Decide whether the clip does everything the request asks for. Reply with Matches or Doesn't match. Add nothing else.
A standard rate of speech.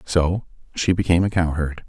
Matches